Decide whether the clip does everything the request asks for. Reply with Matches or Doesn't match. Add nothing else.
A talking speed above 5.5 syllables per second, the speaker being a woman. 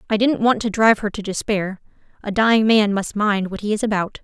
Matches